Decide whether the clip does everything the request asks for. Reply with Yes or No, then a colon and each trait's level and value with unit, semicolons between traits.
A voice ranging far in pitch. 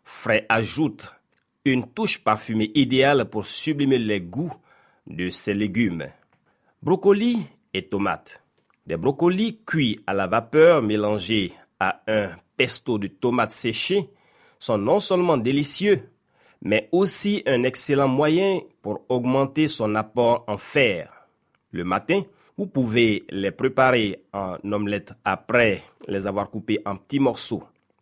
Yes: wide, 6.9 semitones